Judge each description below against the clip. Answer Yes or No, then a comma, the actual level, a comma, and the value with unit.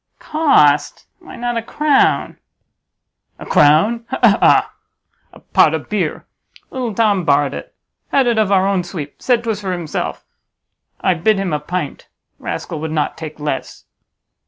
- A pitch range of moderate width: No, wide, 7.2 semitones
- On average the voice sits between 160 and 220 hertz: Yes, high, 190 Hz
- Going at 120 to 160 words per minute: Yes, average, 155 wpm